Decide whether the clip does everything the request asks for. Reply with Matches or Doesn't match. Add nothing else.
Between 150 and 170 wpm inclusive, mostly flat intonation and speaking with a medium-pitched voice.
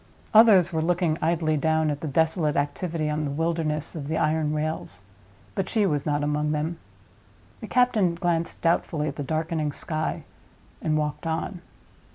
Matches